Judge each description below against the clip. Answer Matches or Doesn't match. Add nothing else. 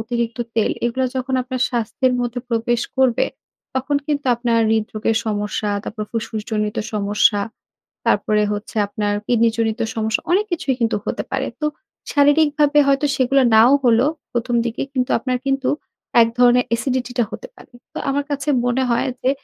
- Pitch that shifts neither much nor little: Matches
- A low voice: Doesn't match